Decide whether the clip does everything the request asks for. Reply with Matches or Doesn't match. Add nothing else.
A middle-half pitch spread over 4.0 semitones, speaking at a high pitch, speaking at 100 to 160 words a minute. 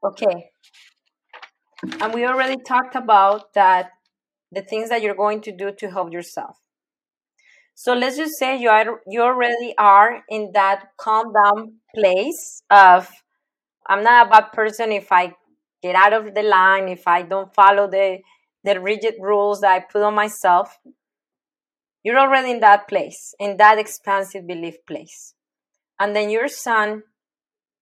Doesn't match